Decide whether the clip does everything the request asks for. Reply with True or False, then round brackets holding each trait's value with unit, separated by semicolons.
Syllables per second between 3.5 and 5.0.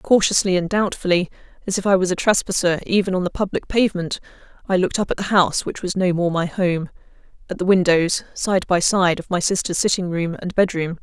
False (5.8 syllables/s)